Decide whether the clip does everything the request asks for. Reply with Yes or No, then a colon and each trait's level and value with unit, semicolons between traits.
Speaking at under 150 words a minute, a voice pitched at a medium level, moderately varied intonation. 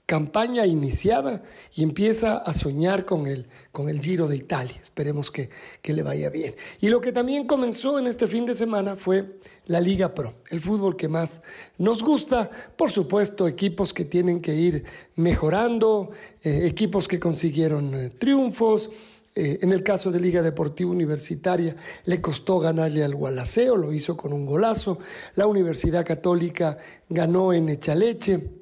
No: average, 160 wpm; medium, 180 Hz; average, 5.0 semitones